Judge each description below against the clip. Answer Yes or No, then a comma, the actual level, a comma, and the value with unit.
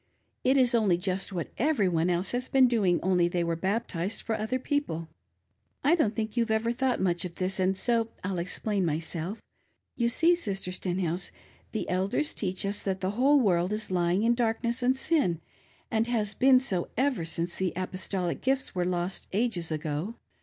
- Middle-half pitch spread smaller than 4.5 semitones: No, average, 5.0 semitones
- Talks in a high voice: Yes, high, 195 Hz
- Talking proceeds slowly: No, average, 185 wpm